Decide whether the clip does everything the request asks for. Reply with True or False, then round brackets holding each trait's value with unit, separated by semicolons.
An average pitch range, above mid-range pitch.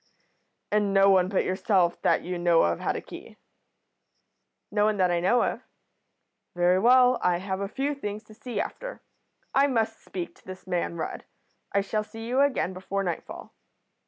True (3.7 semitones; 200 Hz)